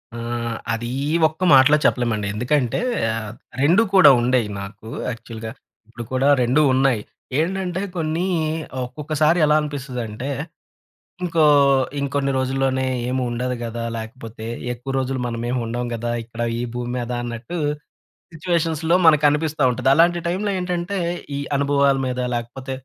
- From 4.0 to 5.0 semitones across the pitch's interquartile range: Yes, average, 4.5 semitones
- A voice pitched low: Yes, low, 130 Hz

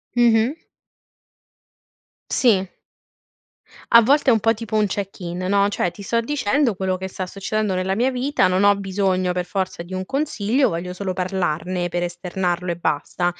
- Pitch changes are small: No, average, 3.5 semitones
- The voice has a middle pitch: No, high, 195 Hz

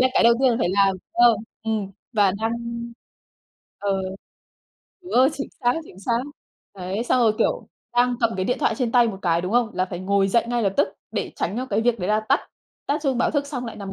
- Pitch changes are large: No, average, 3.8 semitones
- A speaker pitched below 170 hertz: No, high, 225 Hz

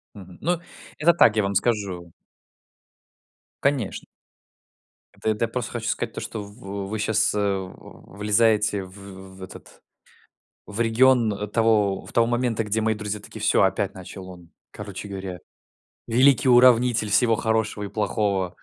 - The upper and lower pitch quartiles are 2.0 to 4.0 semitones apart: Yes, average, 2.7 semitones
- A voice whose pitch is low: Yes, low, 105 Hz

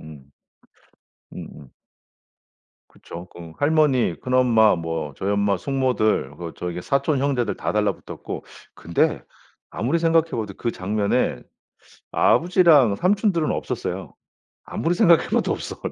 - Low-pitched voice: Yes, low, 115 Hz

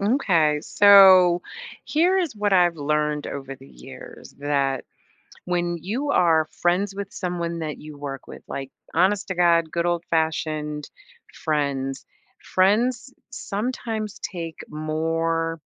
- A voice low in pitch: No, medium, 170 Hz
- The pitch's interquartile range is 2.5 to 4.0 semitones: No, average, 4.5 semitones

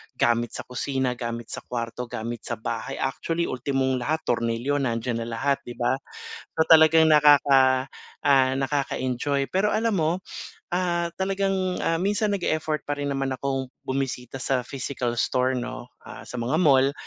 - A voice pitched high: No, low, 135 Hz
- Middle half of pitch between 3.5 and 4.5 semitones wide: Yes, average, 4.1 semitones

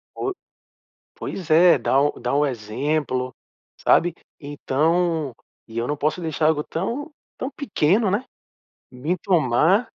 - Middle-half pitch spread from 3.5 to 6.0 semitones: Yes, average, 4.7 semitones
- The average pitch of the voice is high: No, medium, 155 Hz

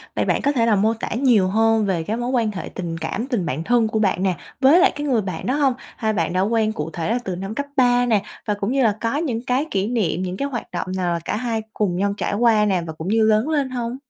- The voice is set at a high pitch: Yes, high, 220 Hz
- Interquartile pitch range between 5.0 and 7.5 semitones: No, average, 4.2 semitones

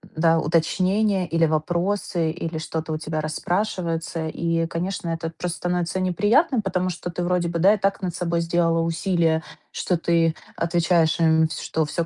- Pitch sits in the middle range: Yes, medium, 170 Hz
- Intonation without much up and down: Yes, narrow, 1.8 semitones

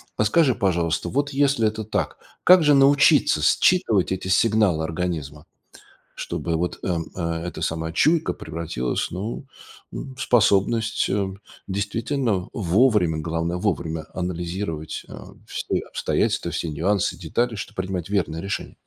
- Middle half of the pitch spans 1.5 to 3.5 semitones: No, wide, 5.6 semitones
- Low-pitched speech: Yes, very low, 95 Hz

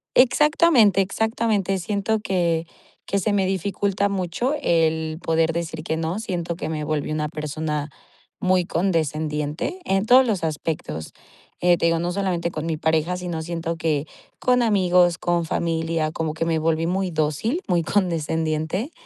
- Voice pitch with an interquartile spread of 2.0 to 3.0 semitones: No, average, 3.4 semitones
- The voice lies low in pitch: No, medium, 170 Hz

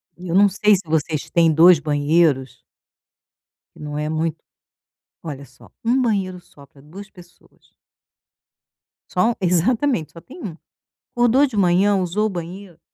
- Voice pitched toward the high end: No, medium, 175 Hz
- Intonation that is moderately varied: Yes, average, 4.5 semitones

